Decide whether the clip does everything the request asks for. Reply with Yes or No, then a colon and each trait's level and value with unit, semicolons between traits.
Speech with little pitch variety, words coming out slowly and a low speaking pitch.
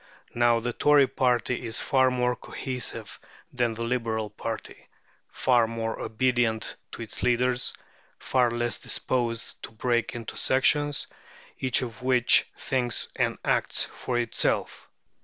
Yes: narrow, 1.6 semitones; slow, 130 wpm; low, 120 Hz